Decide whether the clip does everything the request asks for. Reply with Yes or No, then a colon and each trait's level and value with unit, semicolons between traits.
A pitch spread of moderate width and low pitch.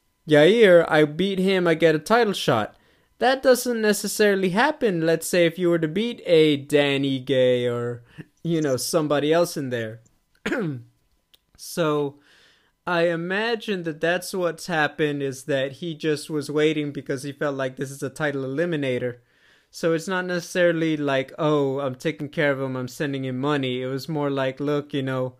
No: average, 3.9 semitones; medium, 150 Hz